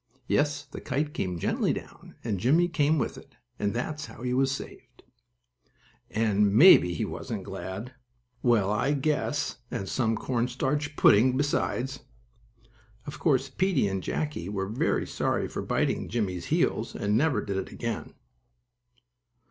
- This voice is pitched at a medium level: No, low, 125 Hz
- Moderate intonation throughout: No, wide, 5.9 semitones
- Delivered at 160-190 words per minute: No, average, 150 wpm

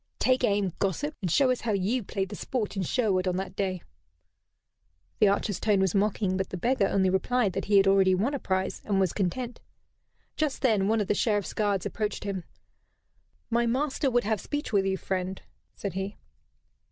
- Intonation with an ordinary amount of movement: Yes, average, 3.3 semitones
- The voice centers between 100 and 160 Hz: No, high, 200 Hz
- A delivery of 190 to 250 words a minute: Yes, average, 195 wpm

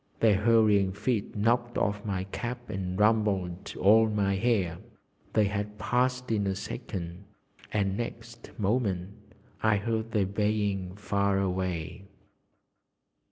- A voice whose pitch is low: Yes, low, 105 Hz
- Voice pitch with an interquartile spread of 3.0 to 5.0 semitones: No, narrow, 2.6 semitones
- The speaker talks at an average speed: No, slow, 120 wpm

